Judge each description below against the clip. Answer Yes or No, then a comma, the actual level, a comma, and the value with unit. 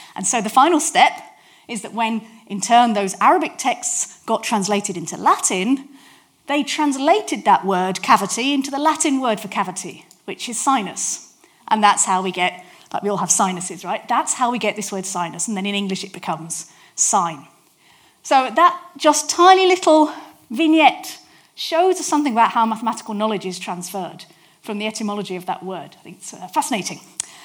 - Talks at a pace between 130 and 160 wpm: No, average, 175 wpm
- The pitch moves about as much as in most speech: No, wide, 7.6 semitones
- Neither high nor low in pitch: No, high, 225 Hz